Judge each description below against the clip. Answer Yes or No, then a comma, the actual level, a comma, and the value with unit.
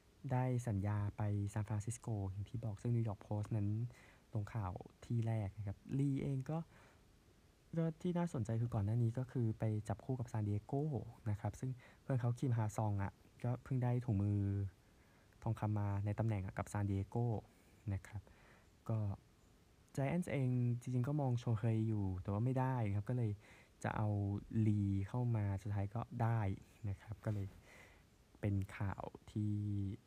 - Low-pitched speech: Yes, low, 110 Hz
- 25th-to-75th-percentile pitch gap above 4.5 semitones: No, average, 2.8 semitones